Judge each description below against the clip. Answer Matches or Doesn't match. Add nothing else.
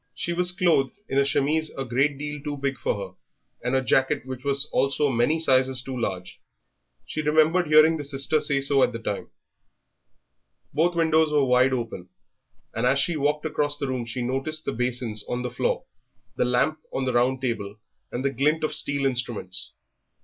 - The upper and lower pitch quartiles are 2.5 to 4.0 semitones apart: Matches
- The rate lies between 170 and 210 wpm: Matches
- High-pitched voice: Doesn't match